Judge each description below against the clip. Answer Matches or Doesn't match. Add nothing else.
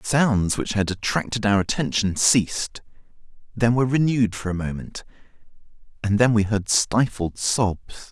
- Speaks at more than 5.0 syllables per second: Doesn't match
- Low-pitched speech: Matches